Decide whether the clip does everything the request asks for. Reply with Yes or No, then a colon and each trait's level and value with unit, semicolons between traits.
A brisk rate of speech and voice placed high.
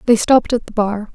Yes: fast, 260 wpm; high, 220 Hz